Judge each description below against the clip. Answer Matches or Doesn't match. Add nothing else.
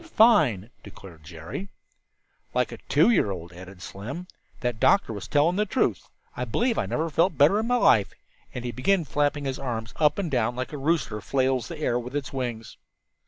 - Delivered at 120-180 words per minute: Doesn't match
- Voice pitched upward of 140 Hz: Doesn't match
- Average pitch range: Doesn't match